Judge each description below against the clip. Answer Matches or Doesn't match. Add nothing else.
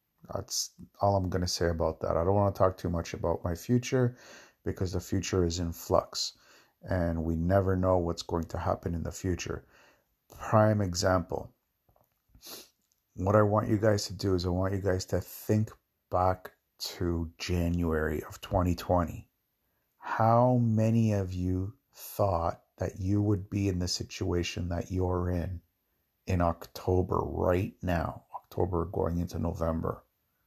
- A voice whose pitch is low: Matches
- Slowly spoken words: Doesn't match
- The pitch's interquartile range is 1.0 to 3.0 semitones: Matches